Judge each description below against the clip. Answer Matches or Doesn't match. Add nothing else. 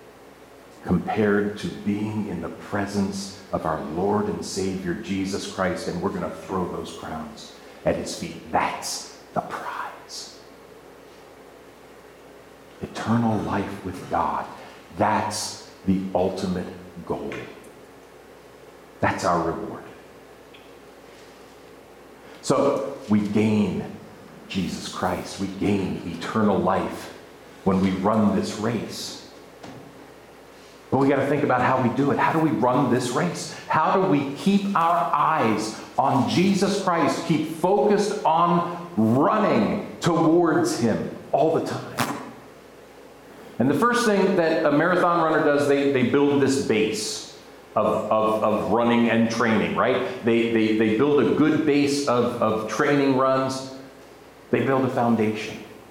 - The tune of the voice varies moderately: Doesn't match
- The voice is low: Matches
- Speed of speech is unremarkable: Doesn't match